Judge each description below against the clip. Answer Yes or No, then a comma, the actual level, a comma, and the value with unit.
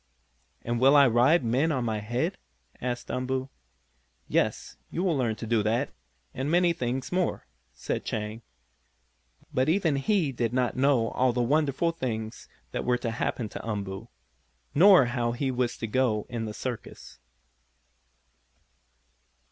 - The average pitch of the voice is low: Yes, low, 125 Hz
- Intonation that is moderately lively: Yes, average, 3.4 semitones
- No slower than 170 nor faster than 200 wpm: No, average, 150 wpm